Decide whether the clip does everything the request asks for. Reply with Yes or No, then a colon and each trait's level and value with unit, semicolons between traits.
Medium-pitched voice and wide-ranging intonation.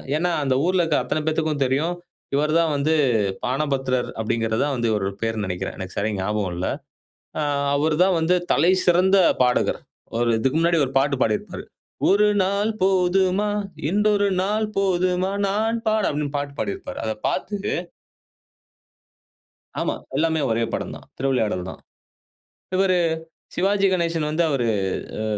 Yes: medium, 160 Hz; wide, 6.6 semitones